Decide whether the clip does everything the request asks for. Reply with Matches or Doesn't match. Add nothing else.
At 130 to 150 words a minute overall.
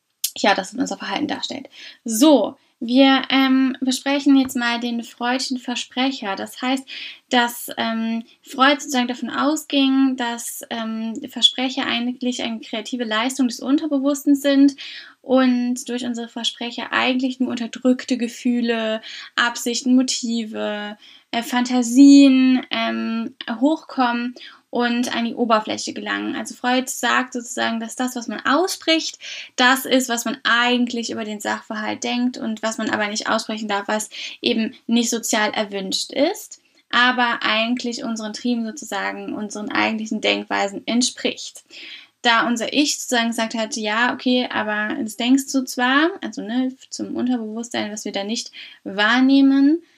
Matches